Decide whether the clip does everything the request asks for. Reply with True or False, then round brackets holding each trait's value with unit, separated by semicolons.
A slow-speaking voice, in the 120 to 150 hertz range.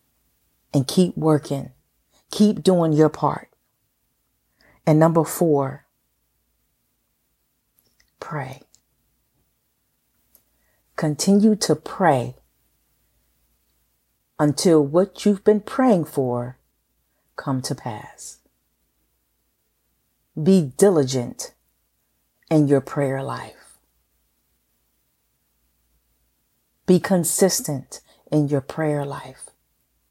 True (70 wpm; 140 Hz)